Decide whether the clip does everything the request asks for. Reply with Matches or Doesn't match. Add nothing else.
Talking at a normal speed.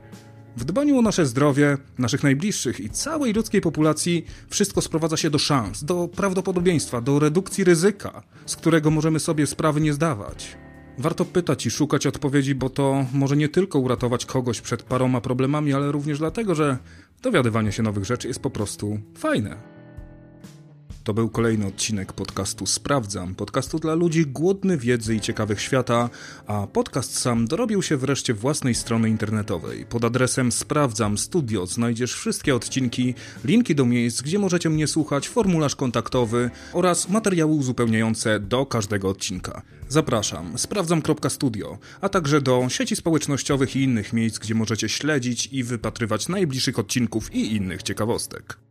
Matches